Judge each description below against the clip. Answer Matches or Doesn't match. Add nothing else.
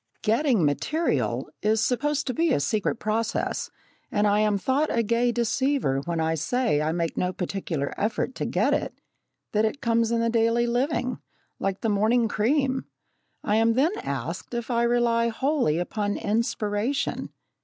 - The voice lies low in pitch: Doesn't match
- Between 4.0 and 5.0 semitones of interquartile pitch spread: Doesn't match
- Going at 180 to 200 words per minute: Doesn't match